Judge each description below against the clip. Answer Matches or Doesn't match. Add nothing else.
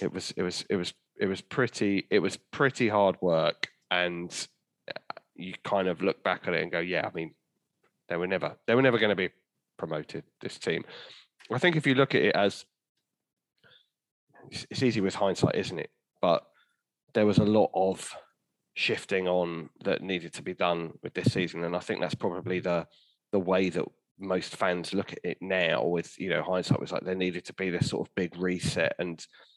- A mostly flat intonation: Matches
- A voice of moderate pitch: Doesn't match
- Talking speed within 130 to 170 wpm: Doesn't match